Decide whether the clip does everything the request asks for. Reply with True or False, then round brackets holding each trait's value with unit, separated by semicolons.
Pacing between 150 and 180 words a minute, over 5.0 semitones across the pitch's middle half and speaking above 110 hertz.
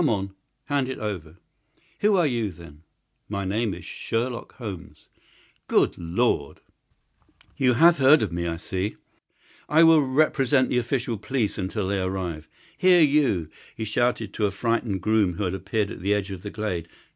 False (170 wpm; 5.6 semitones; 105 Hz)